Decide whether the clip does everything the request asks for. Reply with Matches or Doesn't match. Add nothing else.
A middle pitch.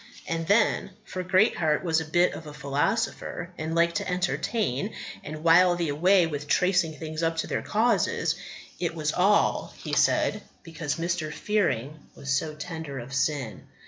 Matches